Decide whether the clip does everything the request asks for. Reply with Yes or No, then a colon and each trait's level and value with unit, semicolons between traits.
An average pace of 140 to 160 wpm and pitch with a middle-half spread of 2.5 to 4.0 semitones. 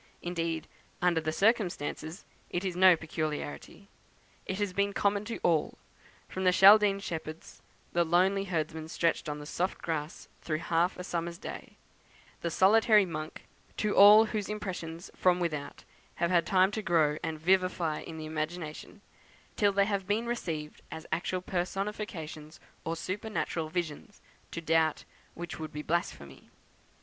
Yes: average, 150 wpm; average, 3.6 semitones